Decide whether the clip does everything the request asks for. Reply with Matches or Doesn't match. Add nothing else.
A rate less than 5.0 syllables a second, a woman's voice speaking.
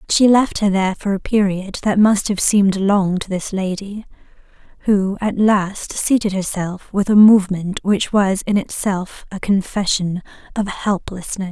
Matches